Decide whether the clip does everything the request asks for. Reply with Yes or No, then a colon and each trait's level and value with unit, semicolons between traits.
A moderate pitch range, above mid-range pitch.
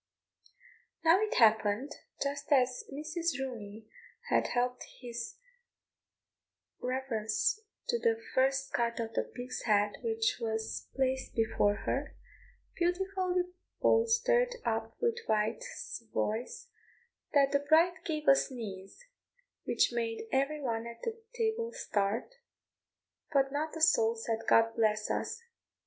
No: wide, 7.1 semitones; very high, 265 Hz